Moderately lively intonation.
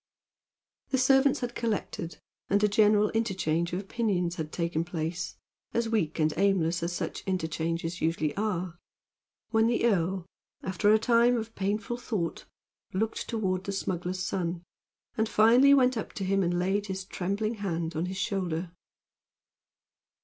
Yes: average, 4.3 semitones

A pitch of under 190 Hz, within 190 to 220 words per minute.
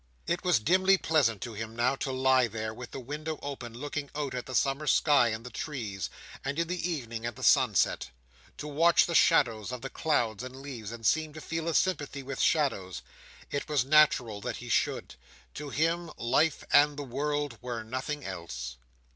Yes: low, 135 Hz; average, 195 wpm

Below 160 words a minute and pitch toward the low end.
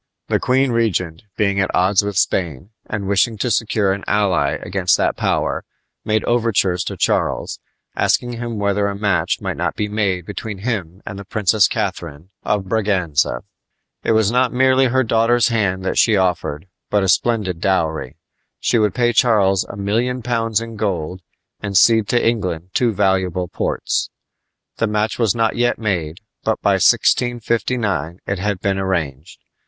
No: average, 165 wpm; low, 100 Hz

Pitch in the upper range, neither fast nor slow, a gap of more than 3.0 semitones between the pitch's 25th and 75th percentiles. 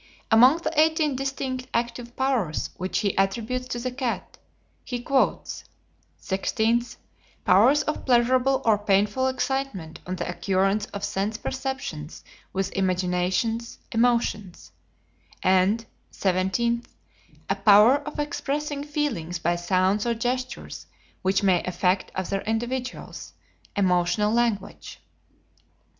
No: high, 225 Hz; slow, 110 wpm; average, 5.2 semitones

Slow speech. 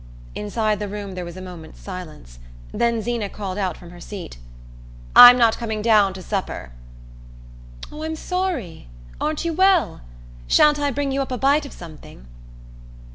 No: average, 165 wpm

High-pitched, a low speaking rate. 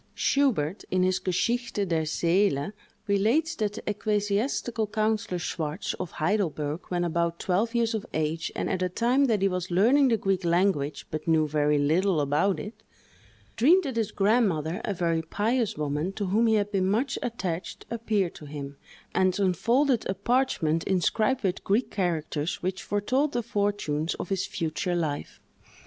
No: high, 195 Hz; average, 165 wpm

